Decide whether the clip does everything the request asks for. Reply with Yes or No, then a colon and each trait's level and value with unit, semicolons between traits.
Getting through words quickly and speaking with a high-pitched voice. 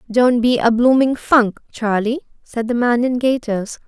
No: average, 170 wpm; high, 240 Hz